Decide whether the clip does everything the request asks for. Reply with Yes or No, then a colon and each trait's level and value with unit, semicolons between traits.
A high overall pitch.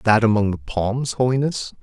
No: low, 110 Hz